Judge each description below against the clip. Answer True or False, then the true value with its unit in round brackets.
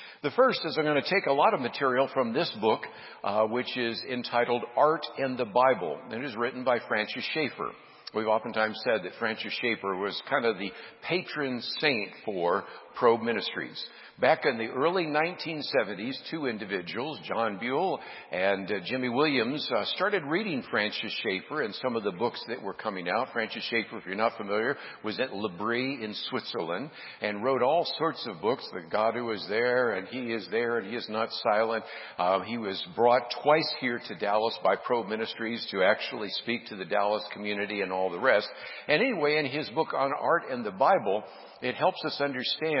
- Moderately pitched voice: False (120 Hz)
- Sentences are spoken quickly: False (195 wpm)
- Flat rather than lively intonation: False (4.4 semitones)